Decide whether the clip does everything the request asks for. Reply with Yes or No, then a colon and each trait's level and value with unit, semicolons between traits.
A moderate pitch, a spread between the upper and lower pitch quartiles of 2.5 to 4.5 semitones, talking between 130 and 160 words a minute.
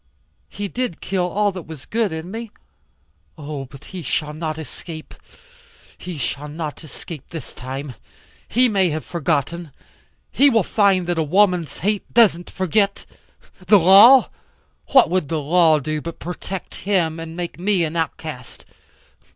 Yes: medium, 170 Hz; average, 4.1 semitones; average, 150 wpm